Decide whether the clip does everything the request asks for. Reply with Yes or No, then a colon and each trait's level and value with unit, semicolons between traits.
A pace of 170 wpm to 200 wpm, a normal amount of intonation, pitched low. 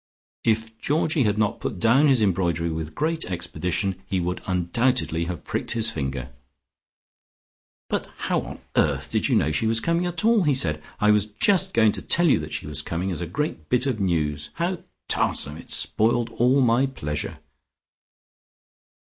No: average, 175 wpm; wide, 7.8 semitones; low, 105 Hz